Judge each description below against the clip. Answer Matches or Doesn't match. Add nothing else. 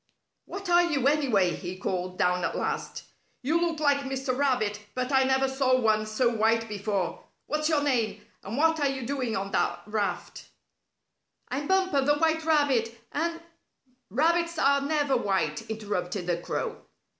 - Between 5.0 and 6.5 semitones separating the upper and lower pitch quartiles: Matches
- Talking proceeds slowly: Doesn't match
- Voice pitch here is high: Matches